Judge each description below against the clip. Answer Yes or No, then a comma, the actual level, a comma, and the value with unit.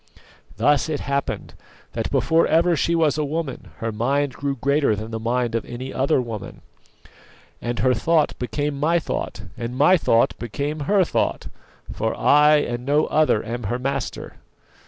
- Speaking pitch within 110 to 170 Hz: Yes, medium, 140 Hz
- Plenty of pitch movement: No, average, 4.1 semitones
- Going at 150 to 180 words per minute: Yes, average, 165 wpm